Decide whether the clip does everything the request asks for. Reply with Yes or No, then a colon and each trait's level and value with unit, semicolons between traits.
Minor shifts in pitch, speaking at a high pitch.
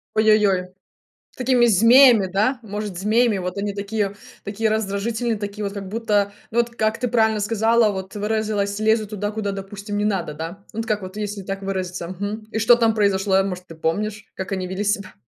Yes: narrow, 2.1 semitones; high, 205 Hz